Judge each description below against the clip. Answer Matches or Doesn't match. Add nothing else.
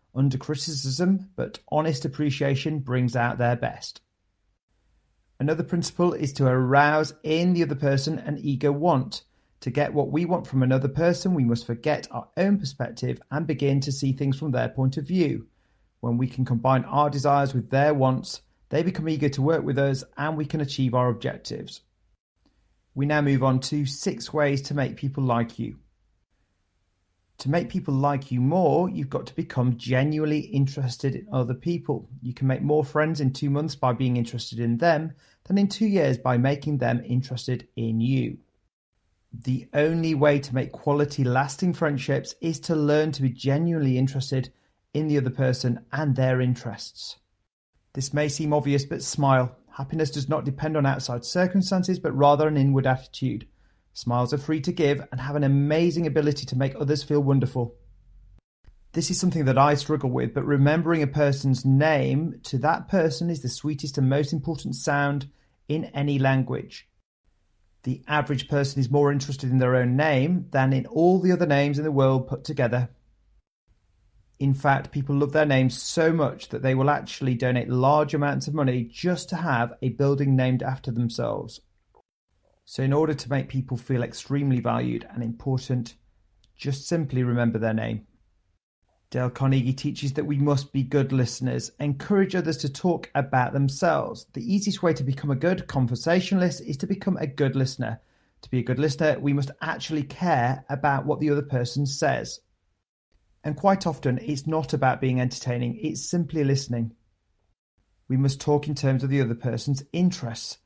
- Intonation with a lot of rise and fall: Doesn't match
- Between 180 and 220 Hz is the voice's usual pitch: Doesn't match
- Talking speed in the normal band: Matches